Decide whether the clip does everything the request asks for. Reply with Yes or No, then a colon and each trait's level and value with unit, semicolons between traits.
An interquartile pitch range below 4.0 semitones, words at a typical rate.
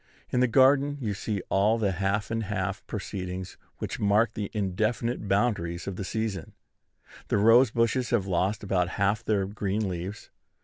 Yes: average, 2.8 semitones; average, 165 wpm